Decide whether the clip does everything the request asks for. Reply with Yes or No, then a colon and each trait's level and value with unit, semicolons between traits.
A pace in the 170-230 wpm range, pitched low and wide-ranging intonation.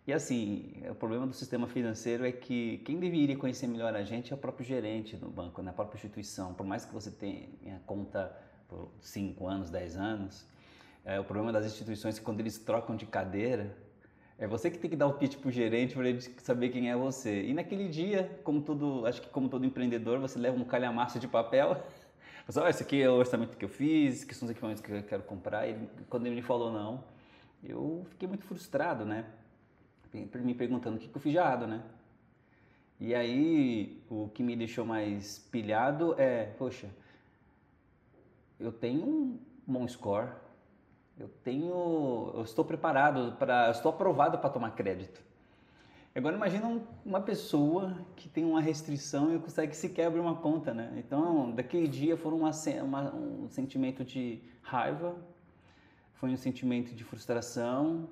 Yes: average, 180 wpm; low, 125 Hz; wide, 5.7 semitones